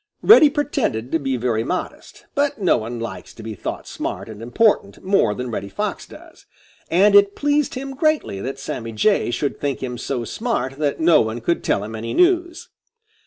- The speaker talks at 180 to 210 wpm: Yes, average, 190 wpm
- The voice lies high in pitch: No, medium, 140 Hz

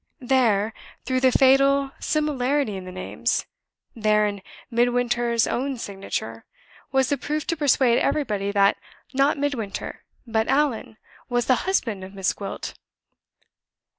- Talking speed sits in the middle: No, slow, 130 wpm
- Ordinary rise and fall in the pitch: Yes, average, 4.8 semitones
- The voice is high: Yes, high, 240 Hz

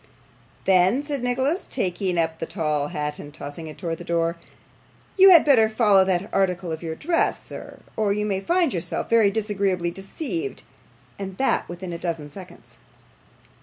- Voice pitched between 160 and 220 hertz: Yes, high, 190 Hz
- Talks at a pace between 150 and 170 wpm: Yes, average, 165 wpm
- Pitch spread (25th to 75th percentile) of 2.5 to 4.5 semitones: No, average, 5.3 semitones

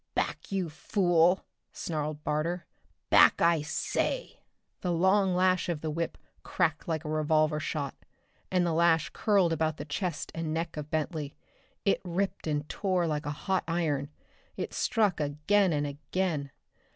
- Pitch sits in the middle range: Yes, medium, 165 Hz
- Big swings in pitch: No, average, 3.1 semitones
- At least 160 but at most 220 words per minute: No, average, 150 wpm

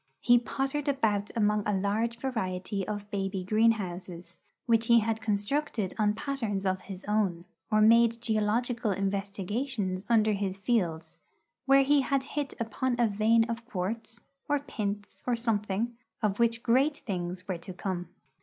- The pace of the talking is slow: No, average, 150 wpm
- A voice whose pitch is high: Yes, high, 215 Hz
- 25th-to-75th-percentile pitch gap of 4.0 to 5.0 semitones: No, average, 3.2 semitones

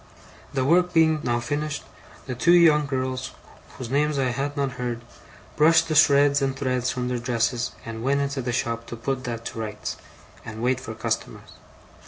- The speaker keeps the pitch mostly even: No, average, 3.1 semitones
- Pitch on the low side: Yes, low, 130 Hz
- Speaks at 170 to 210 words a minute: Yes, average, 180 wpm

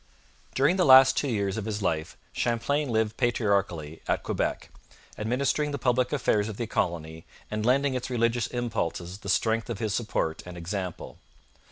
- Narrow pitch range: No, average, 4.3 semitones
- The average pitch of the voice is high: No, low, 110 Hz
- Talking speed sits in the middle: Yes, average, 165 wpm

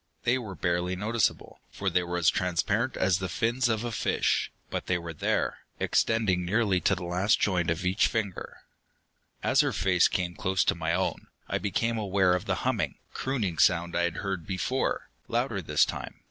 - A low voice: Yes, very low, 95 Hz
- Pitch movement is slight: No, average, 3.7 semitones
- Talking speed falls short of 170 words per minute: No, average, 190 wpm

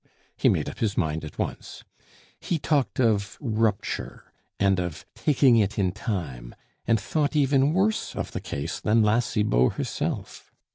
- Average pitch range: No, wide, 6.0 semitones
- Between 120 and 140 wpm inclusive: No, average, 155 wpm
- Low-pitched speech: Yes, low, 110 Hz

